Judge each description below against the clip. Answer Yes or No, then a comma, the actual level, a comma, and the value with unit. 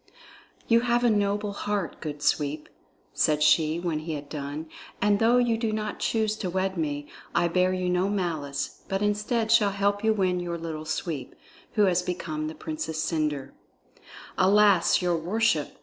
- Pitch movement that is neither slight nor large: Yes, average, 4.8 semitones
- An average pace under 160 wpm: No, average, 170 wpm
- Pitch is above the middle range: No, medium, 180 Hz